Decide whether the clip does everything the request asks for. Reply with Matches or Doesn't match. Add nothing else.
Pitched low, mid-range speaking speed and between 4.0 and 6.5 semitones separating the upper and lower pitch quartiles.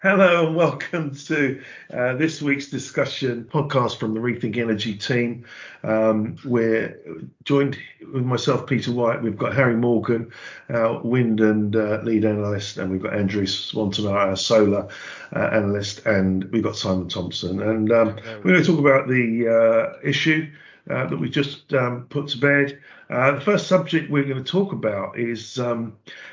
Matches